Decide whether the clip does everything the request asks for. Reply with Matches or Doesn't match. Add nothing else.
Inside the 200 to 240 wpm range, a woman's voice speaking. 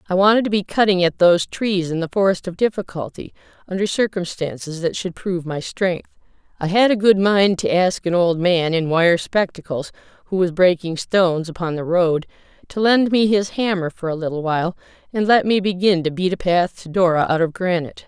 Matches